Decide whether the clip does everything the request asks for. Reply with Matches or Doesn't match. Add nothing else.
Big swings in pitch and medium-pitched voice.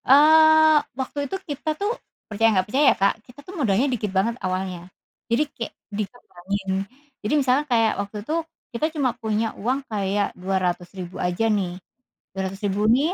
Doesn't match